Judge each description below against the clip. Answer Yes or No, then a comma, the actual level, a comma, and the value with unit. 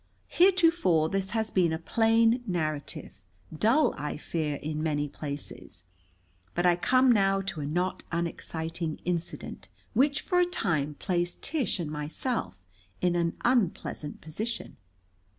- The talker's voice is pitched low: No, medium, 175 Hz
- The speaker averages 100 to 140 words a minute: Yes, slow, 135 wpm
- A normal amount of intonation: No, wide, 6.6 semitones